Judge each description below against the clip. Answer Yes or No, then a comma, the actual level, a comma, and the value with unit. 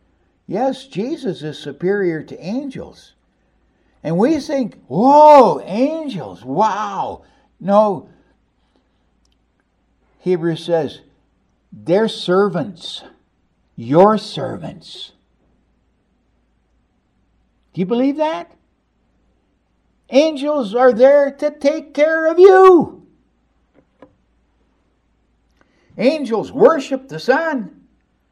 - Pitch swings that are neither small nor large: No, wide, 8.6 semitones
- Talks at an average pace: No, slow, 75 wpm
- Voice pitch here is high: Yes, high, 235 Hz